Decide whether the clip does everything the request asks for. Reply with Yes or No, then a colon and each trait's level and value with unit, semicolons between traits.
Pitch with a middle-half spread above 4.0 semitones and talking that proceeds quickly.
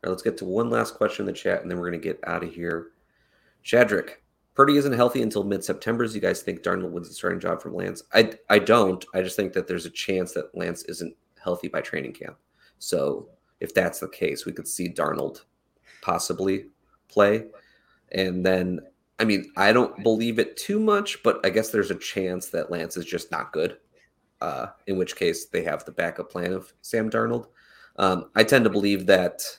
Yes: average, 4.5 semitones; fast, 215 wpm